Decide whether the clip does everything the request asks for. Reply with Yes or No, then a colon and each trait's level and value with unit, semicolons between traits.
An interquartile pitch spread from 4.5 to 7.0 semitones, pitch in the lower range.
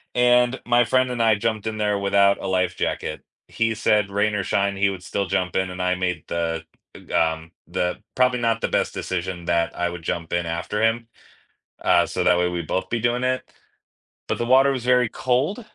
Yes: average, 5.0 semitones; low, 100 Hz